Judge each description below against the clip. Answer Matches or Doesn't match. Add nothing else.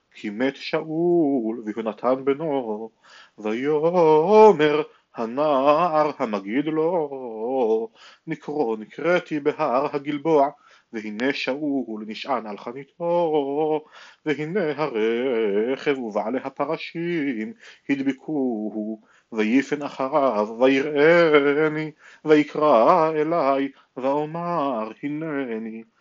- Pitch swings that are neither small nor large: Matches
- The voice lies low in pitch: Doesn't match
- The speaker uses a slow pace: Matches